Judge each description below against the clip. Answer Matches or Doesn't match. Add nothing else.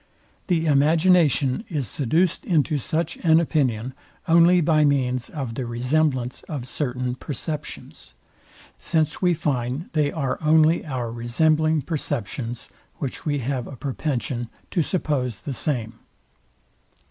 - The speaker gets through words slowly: Matches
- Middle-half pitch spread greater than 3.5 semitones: Matches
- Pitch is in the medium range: Matches